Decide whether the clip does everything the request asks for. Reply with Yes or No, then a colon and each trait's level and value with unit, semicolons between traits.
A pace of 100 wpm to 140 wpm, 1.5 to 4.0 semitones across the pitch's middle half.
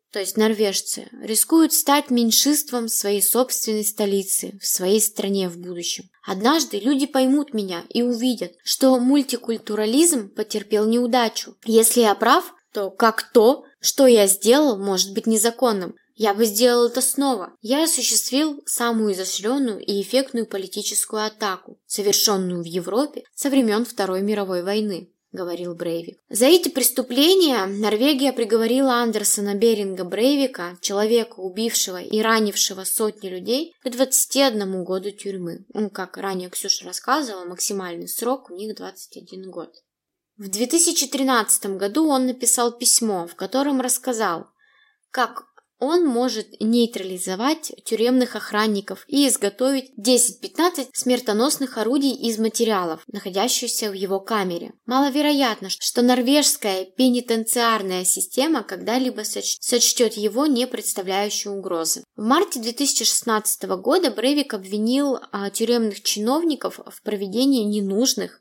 No: average, 120 wpm; average, 4.4 semitones